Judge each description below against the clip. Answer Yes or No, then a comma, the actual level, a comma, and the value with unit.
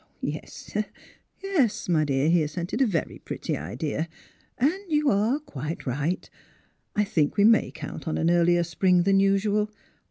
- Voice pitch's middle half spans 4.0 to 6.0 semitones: Yes, average, 5.0 semitones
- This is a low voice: No, medium, 180 Hz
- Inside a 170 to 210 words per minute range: No, average, 160 wpm